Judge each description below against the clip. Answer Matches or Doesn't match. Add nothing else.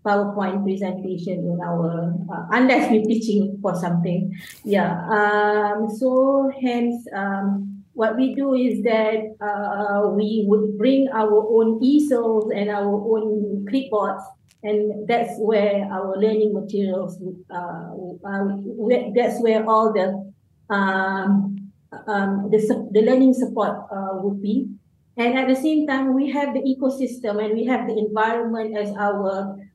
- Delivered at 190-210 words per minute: Doesn't match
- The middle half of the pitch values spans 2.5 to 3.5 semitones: Matches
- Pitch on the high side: Matches